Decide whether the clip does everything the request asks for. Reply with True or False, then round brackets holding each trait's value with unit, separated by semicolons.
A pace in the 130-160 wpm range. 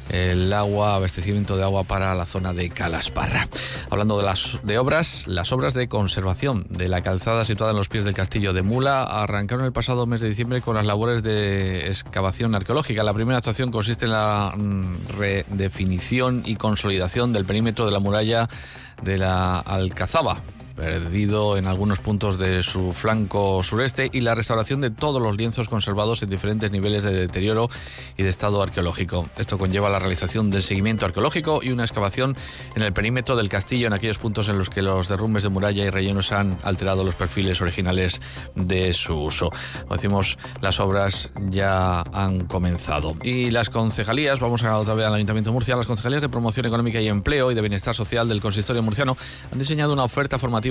False (185 wpm)